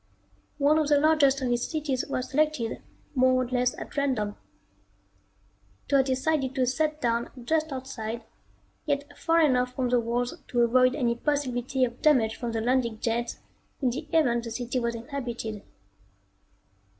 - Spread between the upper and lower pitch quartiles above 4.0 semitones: No, average, 3.2 semitones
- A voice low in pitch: No, very high, 255 Hz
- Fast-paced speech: No, average, 160 wpm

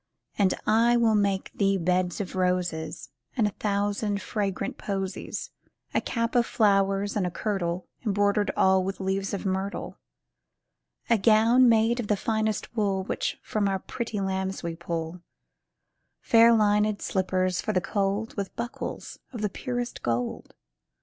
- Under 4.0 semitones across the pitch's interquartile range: Yes, narrow, 2.5 semitones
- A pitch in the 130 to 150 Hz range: No, high, 200 Hz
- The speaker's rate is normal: Yes, average, 150 wpm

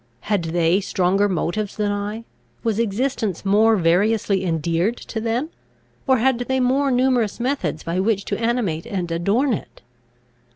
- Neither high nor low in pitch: No, high, 210 Hz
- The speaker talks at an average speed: Yes, average, 150 wpm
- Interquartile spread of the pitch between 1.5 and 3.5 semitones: No, average, 4.4 semitones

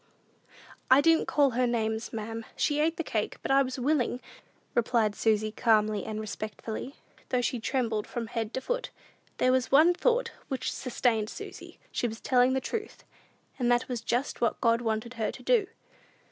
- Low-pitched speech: No, high, 245 Hz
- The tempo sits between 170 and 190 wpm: Yes, average, 175 wpm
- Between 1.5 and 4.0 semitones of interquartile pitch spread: Yes, average, 3.4 semitones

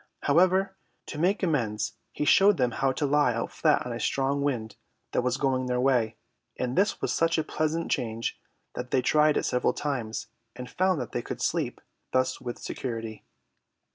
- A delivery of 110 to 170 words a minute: No, average, 185 wpm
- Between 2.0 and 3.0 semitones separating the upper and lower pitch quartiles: No, average, 4.1 semitones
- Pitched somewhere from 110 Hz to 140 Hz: Yes, low, 135 Hz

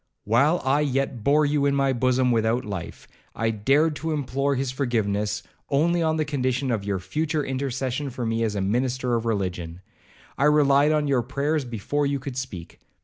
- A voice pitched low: Yes, low, 130 Hz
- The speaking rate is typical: Yes, average, 185 wpm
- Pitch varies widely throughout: No, average, 4.0 semitones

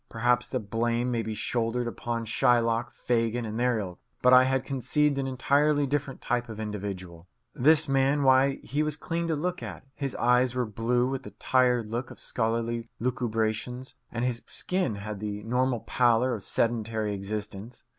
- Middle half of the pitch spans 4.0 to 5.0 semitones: No, average, 2.7 semitones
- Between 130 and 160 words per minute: No, average, 175 wpm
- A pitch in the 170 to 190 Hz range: No, low, 120 Hz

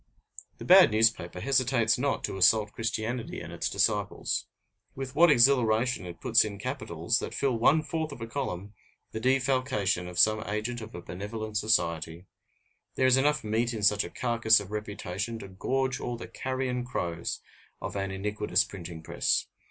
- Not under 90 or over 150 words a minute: No, average, 165 wpm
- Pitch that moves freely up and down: No, average, 4.3 semitones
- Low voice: Yes, low, 110 Hz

